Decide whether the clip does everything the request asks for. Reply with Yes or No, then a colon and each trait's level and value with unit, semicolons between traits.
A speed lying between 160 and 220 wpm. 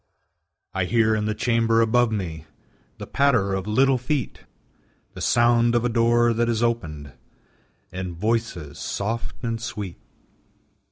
No: slow, 135 wpm